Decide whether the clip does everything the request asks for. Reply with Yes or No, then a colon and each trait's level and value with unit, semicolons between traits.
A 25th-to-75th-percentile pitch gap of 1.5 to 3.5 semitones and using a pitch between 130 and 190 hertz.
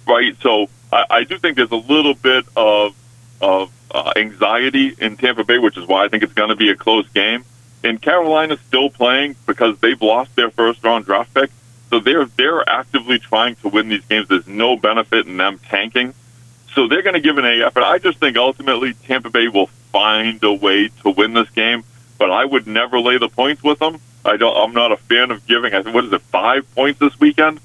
No: average, 2.8 semitones; low, 120 Hz